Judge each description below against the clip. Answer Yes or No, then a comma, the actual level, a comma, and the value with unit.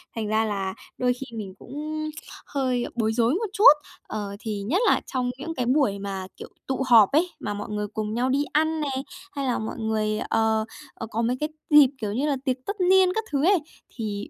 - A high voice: Yes, high, 245 Hz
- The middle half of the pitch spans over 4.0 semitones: Yes, average, 5.2 semitones